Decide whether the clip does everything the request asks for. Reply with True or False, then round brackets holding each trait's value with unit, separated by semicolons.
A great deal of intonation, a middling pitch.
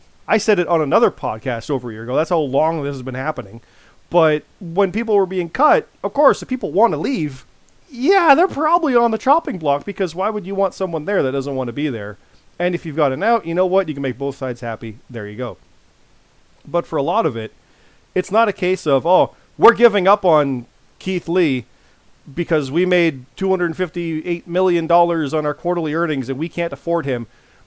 True (5.7 semitones; 170 Hz)